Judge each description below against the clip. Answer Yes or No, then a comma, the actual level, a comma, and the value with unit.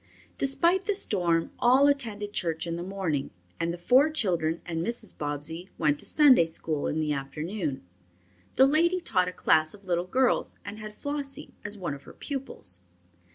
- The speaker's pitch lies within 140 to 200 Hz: Yes, medium, 185 Hz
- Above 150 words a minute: Yes, average, 175 wpm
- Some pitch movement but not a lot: No, wide, 8.5 semitones